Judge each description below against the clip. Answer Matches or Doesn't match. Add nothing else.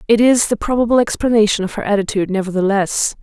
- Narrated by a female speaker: Matches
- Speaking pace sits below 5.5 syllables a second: Doesn't match